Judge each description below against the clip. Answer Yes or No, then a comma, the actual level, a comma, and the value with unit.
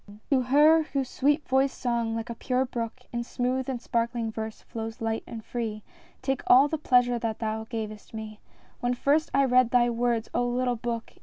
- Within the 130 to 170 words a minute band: No, average, 200 wpm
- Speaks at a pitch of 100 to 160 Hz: No, high, 240 Hz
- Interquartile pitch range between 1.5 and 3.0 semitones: Yes, narrow, 2.4 semitones